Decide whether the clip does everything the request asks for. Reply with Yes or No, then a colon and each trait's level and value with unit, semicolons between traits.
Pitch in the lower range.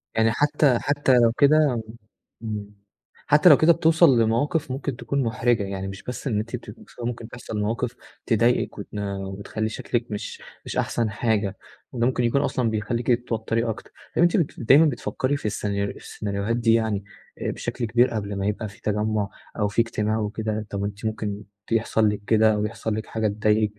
Yes: low, 115 Hz